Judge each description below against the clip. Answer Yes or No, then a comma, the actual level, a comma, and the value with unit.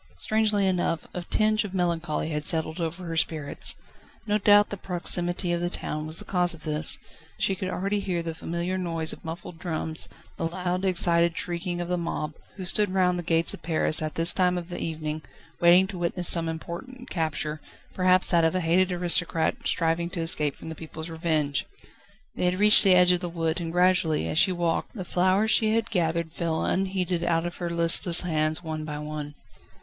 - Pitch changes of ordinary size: No, narrow, 2.1 semitones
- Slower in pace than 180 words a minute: No, average, 200 wpm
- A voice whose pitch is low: No, medium, 175 Hz